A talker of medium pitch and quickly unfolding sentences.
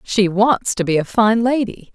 No: high, 210 Hz; fast, 215 wpm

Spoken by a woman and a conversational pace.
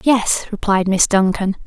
Yes: female; average, 145 wpm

